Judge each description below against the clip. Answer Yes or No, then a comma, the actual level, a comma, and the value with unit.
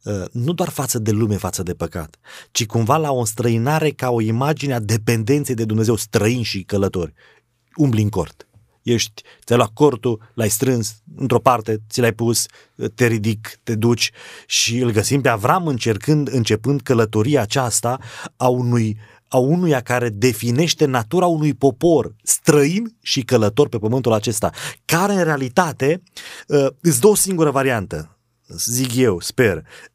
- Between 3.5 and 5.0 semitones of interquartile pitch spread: Yes, average, 4.3 semitones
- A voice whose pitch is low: Yes, low, 120 Hz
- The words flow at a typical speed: Yes, average, 150 wpm